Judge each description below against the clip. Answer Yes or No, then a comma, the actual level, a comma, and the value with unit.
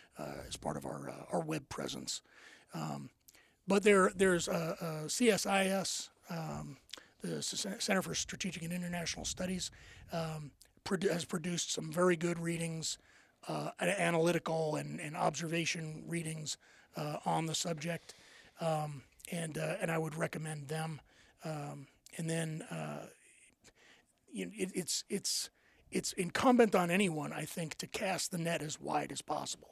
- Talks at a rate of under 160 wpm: Yes, average, 145 wpm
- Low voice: No, medium, 170 Hz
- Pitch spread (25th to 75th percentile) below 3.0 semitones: Yes, narrow, 2.6 semitones